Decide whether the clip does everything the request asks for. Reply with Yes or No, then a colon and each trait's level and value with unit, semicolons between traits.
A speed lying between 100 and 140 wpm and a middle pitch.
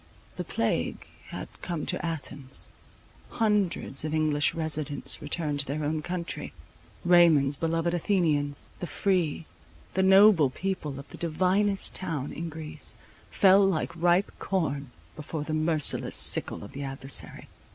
Yes: slow, 135 wpm; medium, 160 Hz